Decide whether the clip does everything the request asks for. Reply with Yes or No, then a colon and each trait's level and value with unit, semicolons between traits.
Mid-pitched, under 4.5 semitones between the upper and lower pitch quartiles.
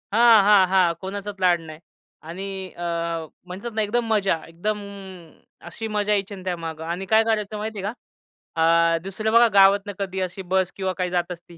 No: high, 195 Hz; average, 2.9 semitones